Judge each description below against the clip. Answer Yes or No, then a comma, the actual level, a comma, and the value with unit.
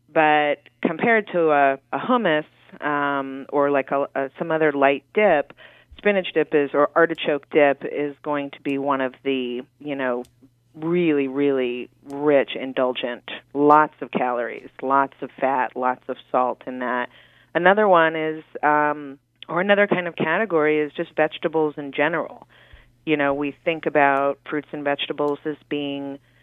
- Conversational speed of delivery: Yes, average, 155 wpm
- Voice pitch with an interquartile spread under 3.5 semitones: Yes, narrow, 2.4 semitones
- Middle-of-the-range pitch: Yes, medium, 145 Hz